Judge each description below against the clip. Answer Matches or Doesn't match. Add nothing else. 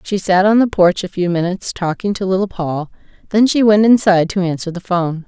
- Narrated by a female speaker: Matches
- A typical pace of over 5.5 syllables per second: Matches